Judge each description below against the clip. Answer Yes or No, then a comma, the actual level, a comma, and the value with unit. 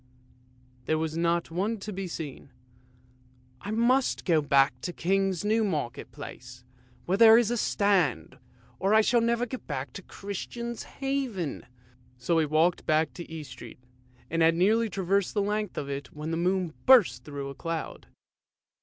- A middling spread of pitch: No, wide, 6.7 semitones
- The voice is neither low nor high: Yes, medium, 170 Hz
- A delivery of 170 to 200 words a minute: Yes, average, 180 wpm